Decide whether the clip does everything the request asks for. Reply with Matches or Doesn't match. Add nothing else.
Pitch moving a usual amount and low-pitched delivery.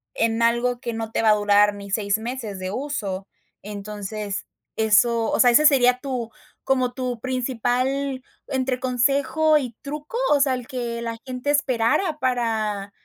Doesn't match